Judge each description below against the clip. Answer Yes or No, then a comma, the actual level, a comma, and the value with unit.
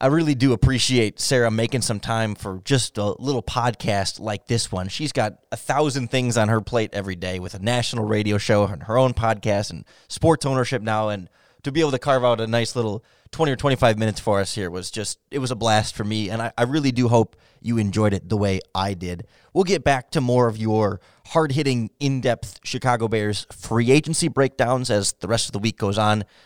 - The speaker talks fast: Yes, fast, 230 wpm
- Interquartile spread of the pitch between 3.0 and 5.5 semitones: Yes, average, 3.8 semitones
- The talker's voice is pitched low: Yes, low, 115 Hz